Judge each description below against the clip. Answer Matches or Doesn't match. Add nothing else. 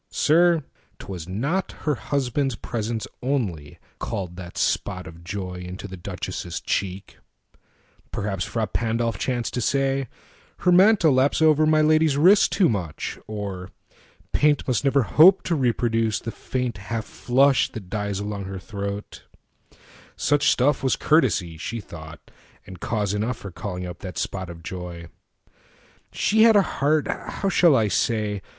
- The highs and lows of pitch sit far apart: Matches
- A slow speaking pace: Matches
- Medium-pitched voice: Doesn't match